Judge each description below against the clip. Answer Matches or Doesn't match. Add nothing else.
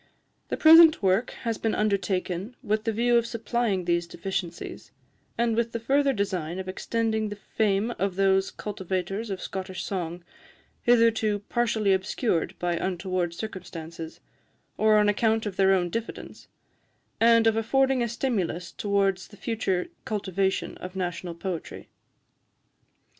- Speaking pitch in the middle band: Doesn't match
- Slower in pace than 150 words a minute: Matches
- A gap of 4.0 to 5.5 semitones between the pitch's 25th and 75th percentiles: Doesn't match